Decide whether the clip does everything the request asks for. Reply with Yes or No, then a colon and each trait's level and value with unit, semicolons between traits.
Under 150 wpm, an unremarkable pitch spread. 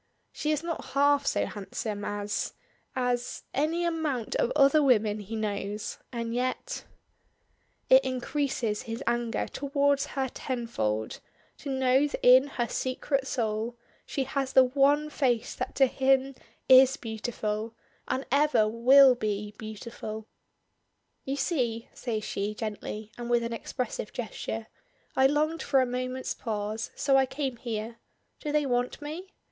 Yes: average, 140 wpm; average, 3.7 semitones